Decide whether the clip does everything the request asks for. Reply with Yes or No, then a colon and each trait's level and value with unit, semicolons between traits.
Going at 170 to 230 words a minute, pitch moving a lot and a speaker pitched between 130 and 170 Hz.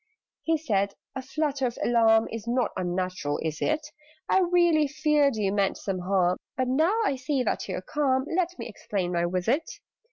No: average, 185 wpm; wide, 7.6 semitones; high, 240 Hz